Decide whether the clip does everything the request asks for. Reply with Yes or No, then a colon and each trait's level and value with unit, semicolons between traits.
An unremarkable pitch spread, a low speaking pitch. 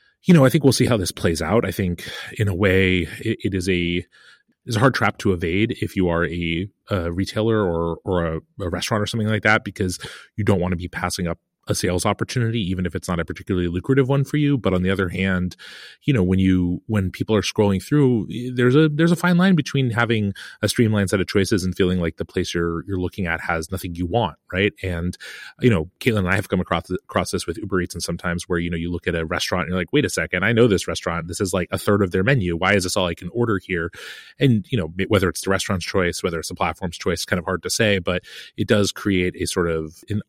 Yes: average, 3.4 semitones; very low, 95 Hz